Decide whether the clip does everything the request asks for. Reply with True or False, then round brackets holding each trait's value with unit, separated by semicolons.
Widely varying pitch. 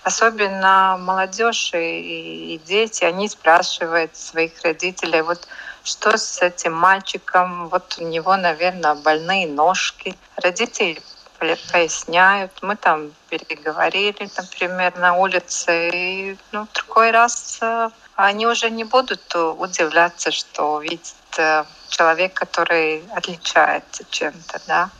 False (3.2 semitones)